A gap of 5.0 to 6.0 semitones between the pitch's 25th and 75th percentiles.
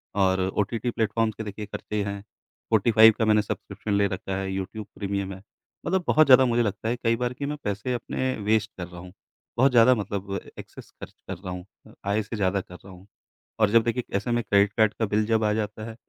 No: average, 2.7 semitones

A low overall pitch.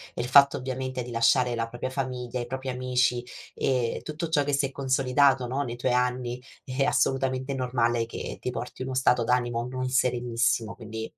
Yes: low, 125 Hz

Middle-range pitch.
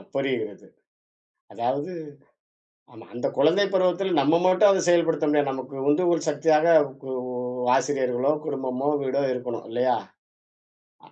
Yes: medium, 145 Hz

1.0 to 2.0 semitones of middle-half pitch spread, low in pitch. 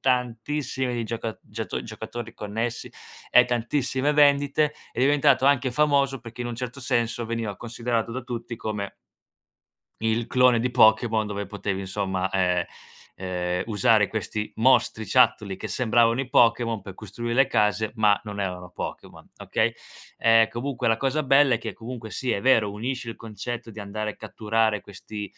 No: average, 2.9 semitones; low, 115 Hz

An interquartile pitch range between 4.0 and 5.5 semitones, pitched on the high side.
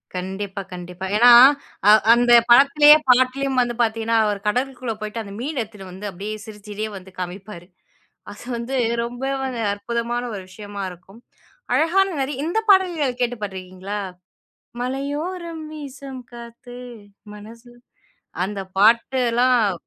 Yes: average, 4.4 semitones; high, 235 Hz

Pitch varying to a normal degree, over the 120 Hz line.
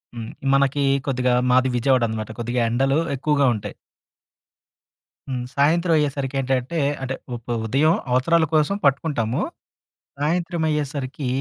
Yes: average, 3.0 semitones; low, 135 Hz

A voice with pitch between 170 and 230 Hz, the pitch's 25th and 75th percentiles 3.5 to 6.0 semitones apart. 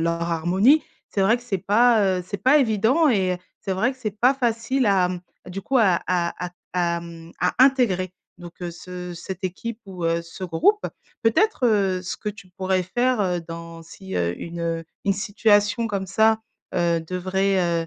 Yes: high, 190 Hz; average, 4.2 semitones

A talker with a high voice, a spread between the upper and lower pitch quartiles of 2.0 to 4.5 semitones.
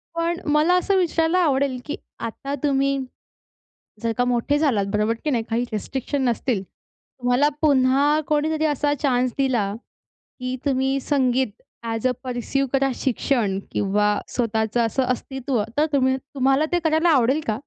Yes: very high, 265 Hz; average, 3.5 semitones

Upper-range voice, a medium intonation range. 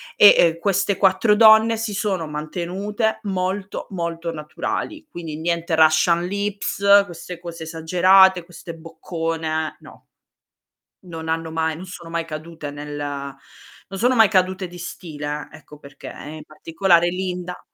No: medium, 170 Hz; average, 3.1 semitones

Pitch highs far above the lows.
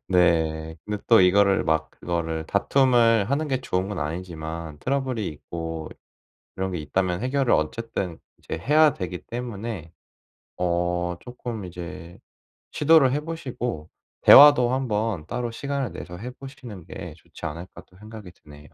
Yes: wide, 6.5 semitones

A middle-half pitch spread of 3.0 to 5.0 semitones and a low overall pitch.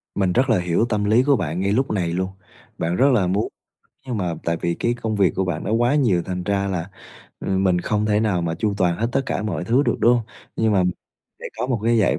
Yes: average, 4.2 semitones; low, 100 Hz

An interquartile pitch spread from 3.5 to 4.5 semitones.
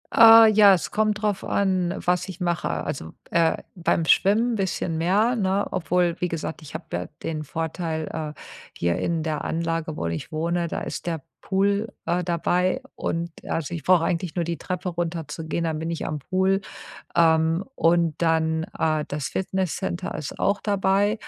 No: average, 2.9 semitones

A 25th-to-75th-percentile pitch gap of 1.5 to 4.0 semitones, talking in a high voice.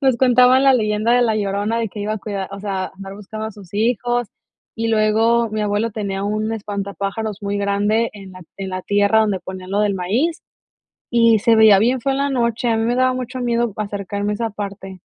Yes: narrow, 2.6 semitones; high, 215 Hz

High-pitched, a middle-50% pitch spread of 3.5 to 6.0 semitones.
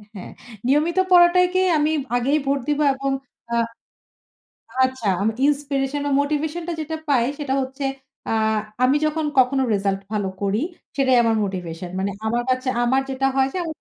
Yes: very high, 270 Hz; average, 4.0 semitones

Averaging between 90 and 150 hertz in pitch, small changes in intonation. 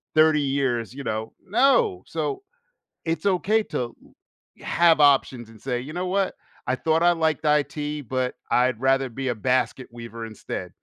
No: medium, 140 Hz; average, 4.8 semitones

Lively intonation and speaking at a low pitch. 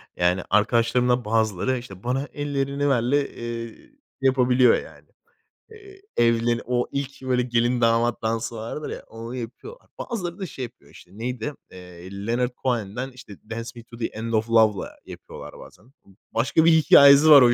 No: average, 3.0 semitones; low, 120 Hz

